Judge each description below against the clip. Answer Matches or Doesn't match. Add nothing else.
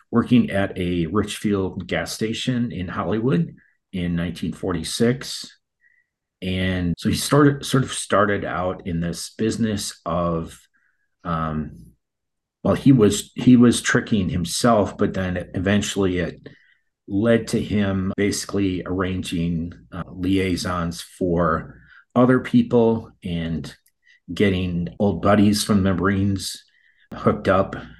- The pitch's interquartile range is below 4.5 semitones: Matches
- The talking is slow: Matches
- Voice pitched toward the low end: Matches